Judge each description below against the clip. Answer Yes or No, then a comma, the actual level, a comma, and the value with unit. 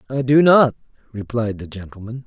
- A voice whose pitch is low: Yes, low, 125 Hz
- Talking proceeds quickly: No, average, 160 wpm